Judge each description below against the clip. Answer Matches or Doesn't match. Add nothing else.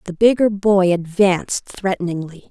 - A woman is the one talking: Matches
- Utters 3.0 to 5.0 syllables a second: Matches